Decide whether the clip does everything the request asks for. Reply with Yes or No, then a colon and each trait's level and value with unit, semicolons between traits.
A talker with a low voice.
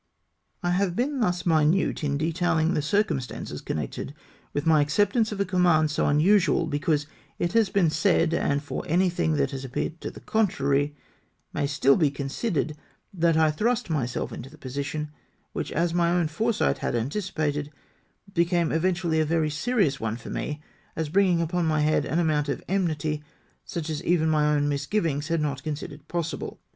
No: medium, 160 Hz